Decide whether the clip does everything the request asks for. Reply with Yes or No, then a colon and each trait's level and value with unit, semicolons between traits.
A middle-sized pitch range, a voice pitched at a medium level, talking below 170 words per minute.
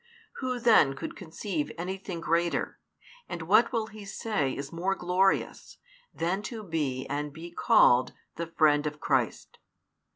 Yes: average, 4.8 semitones; medium, 170 Hz; average, 150 wpm